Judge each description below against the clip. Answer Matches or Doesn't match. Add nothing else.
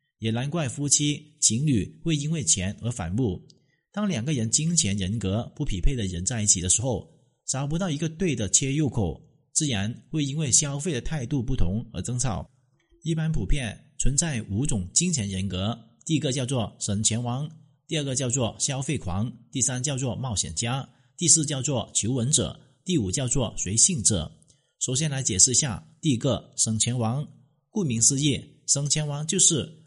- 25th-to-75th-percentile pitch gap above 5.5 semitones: Doesn't match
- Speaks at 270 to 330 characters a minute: Doesn't match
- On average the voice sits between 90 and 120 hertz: Doesn't match